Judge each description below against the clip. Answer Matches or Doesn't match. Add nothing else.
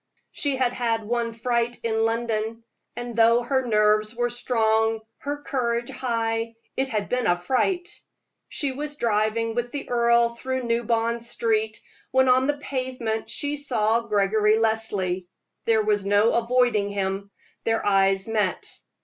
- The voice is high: Matches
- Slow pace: Doesn't match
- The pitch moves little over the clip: Matches